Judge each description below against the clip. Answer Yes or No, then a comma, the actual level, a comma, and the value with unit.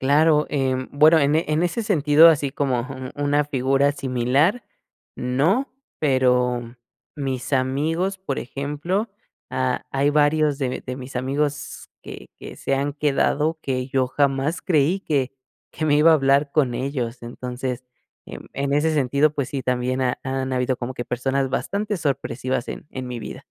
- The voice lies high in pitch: No, medium, 140 Hz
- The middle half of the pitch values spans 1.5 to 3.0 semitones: Yes, average, 2.7 semitones